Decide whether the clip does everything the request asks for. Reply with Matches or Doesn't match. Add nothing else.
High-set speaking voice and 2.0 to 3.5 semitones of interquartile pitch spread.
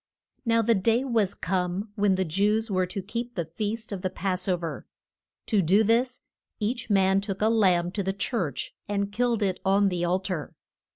Matches